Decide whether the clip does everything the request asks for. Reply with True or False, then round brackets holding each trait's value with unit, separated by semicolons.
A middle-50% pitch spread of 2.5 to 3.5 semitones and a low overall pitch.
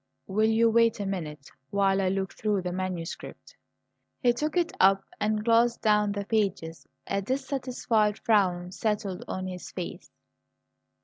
False (3.1 semitones; 205 Hz)